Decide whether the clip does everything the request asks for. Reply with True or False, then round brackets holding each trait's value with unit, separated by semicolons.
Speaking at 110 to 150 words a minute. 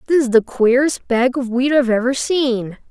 False (205 wpm)